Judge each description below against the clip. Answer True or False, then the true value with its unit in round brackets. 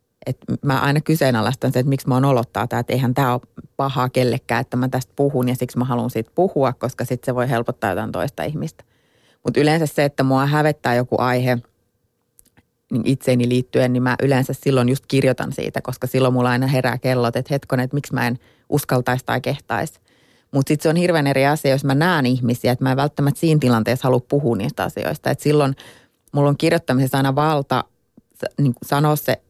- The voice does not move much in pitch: True (2.2 semitones)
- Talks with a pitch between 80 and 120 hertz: False (130 Hz)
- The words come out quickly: True (200 wpm)